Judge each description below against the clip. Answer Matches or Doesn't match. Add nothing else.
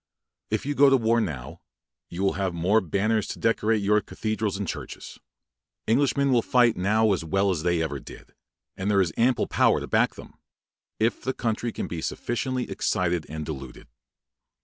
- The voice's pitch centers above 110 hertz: Doesn't match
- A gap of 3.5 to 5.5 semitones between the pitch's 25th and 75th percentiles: Matches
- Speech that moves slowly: Doesn't match